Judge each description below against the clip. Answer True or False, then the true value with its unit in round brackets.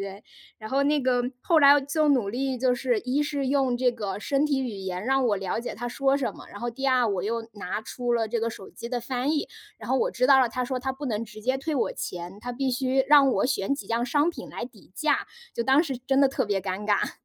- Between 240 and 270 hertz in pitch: True (250 Hz)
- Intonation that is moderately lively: True (3.6 semitones)